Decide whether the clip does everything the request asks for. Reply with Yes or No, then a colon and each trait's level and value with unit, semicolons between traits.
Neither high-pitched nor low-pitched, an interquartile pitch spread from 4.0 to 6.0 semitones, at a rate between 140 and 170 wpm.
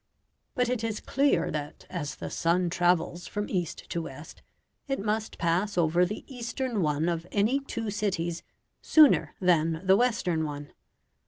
Yes: medium, 180 Hz; average, 5.0 semitones; average, 155 wpm